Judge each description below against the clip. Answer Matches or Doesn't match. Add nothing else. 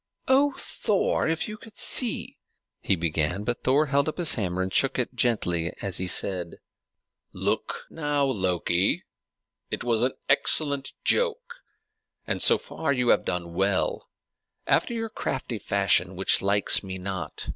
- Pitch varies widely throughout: Matches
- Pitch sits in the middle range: Doesn't match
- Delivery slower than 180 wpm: Matches